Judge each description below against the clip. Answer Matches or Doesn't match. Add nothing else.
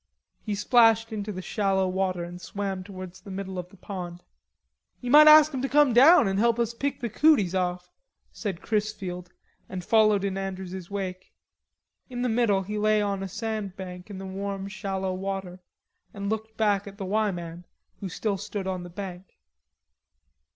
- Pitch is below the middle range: Doesn't match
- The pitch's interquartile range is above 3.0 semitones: Doesn't match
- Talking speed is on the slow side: Doesn't match